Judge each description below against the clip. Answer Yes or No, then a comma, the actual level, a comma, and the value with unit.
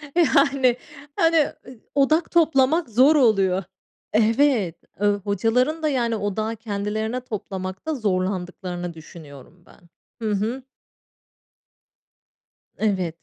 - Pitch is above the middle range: Yes, high, 220 Hz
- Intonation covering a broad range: Yes, wide, 6.1 semitones